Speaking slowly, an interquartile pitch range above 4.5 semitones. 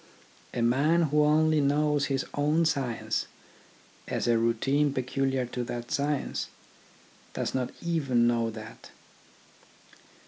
No: slow, 115 wpm; average, 3.7 semitones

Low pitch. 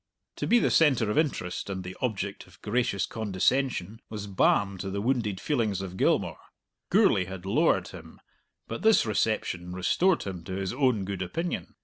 Yes: low, 100 Hz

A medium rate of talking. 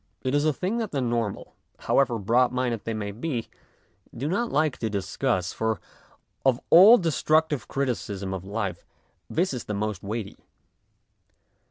Yes: average, 150 wpm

